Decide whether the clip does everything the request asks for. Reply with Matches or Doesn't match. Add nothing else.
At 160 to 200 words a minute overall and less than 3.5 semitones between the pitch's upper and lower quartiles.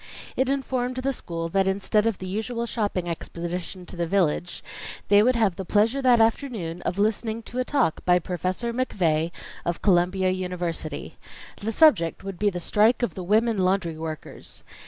Doesn't match